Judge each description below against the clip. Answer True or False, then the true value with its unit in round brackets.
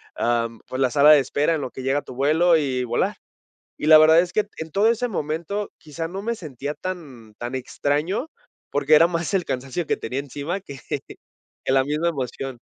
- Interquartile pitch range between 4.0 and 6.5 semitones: True (4.3 semitones)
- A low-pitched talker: False (150 Hz)